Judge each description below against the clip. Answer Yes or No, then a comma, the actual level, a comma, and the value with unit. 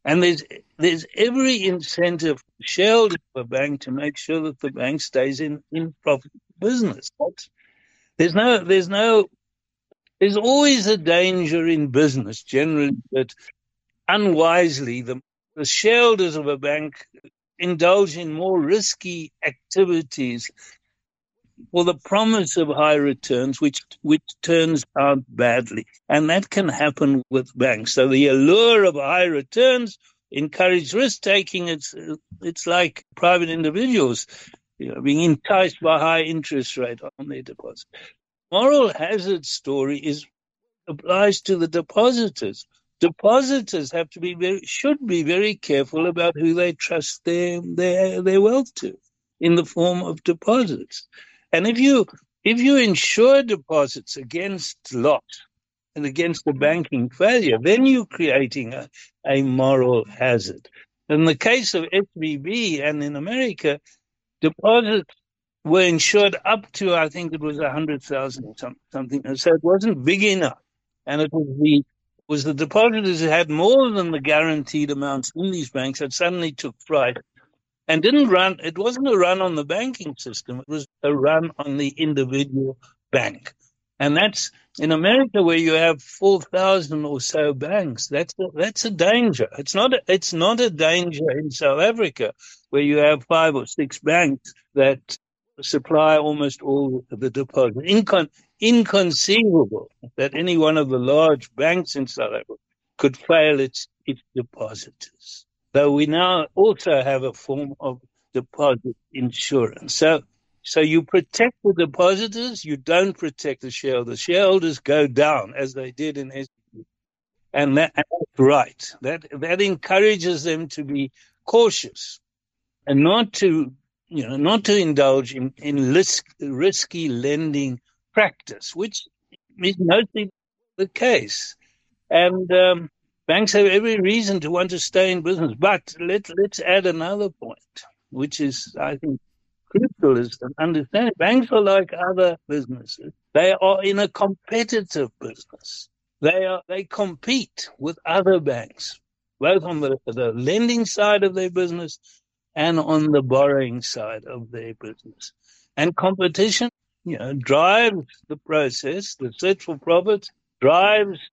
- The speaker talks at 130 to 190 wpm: Yes, average, 145 wpm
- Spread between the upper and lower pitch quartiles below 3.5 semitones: No, wide, 5.5 semitones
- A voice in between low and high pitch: Yes, medium, 165 Hz